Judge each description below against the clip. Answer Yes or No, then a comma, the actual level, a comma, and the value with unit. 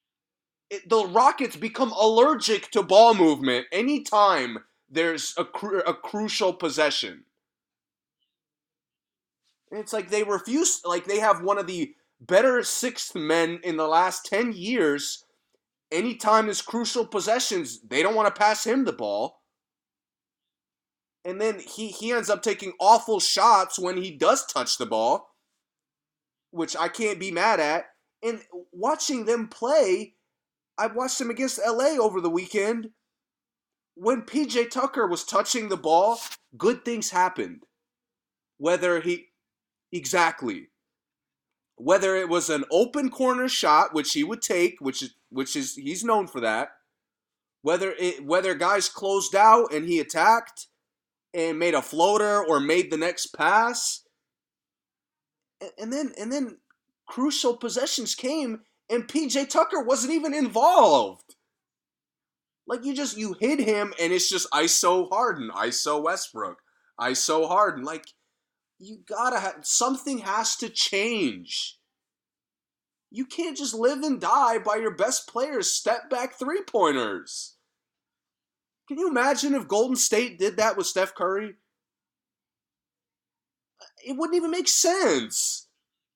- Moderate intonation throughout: No, wide, 6.3 semitones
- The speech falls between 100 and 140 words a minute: Yes, slow, 135 wpm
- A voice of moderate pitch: No, high, 220 Hz